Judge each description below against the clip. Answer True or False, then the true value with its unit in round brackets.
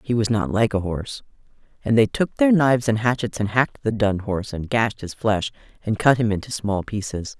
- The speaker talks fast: True (225 wpm)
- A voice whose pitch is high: False (110 Hz)